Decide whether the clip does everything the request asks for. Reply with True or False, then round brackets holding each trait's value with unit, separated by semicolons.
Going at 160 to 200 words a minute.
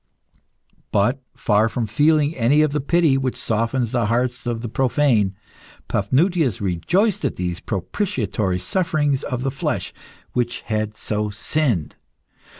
False (135 wpm)